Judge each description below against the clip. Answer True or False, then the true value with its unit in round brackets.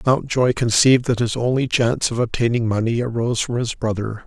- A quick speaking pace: False (185 wpm)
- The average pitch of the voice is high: False (120 Hz)